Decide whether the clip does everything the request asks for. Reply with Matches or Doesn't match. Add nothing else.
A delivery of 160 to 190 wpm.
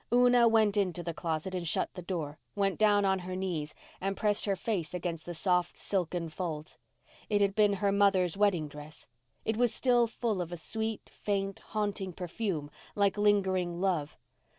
Matches